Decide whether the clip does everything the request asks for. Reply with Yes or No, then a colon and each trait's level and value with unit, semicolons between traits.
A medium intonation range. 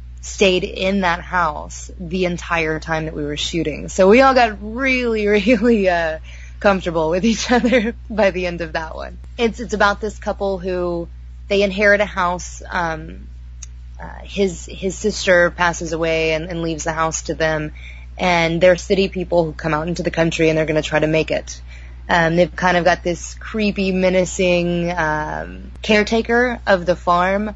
Yes: average, 4.0 semitones